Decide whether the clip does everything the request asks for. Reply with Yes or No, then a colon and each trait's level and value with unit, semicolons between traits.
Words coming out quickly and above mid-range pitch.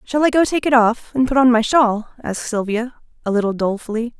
Yes: fast, 230 wpm; high, 235 Hz